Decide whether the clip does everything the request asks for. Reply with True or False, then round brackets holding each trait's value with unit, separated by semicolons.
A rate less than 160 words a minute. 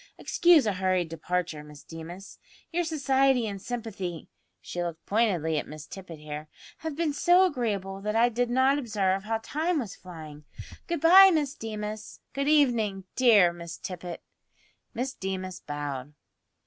True (150 wpm)